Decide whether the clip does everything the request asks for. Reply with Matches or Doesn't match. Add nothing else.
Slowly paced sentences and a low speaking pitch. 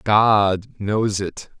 Matches